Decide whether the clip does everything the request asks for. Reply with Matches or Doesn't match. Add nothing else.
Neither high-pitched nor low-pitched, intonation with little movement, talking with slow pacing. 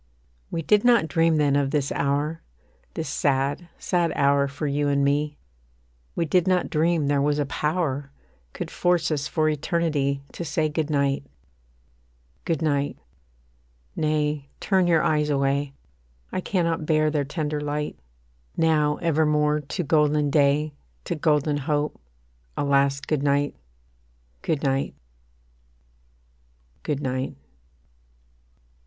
Matches